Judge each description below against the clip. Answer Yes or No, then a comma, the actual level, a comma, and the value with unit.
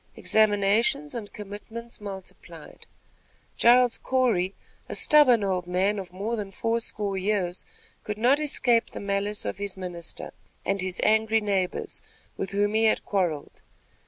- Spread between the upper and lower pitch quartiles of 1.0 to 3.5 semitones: Yes, average, 2.9 semitones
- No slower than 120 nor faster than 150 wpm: Yes, average, 140 wpm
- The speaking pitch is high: Yes, high, 205 Hz